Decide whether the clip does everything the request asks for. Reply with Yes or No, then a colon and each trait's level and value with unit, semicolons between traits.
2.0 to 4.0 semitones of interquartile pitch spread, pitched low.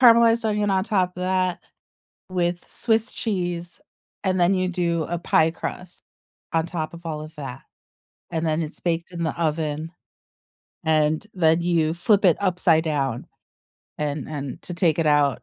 No: average, 2.8 semitones; medium, 170 Hz